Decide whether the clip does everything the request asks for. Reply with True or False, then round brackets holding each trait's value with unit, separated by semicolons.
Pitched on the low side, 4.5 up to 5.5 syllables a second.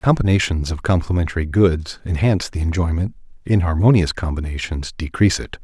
False (85 Hz; 5.7 syllables/s)